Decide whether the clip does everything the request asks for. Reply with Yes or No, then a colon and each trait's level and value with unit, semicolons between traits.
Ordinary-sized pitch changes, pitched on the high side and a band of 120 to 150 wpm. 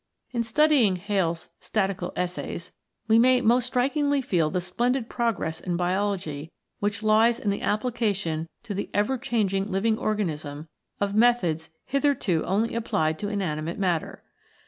Yes: average, 4.8 semitones; high, 205 Hz; average, 140 wpm